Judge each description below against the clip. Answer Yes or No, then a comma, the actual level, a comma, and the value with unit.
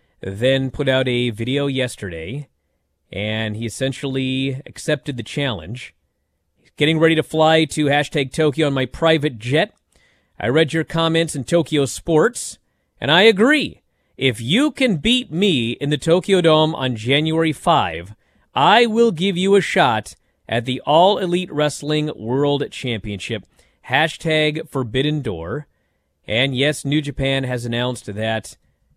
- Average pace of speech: Yes, average, 145 wpm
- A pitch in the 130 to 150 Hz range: Yes, low, 135 Hz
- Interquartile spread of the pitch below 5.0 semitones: No, average, 5.3 semitones